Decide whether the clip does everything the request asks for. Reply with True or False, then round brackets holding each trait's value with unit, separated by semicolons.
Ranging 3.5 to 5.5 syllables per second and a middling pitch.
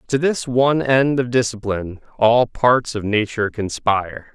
False (4.7 syllables/s; 120 Hz)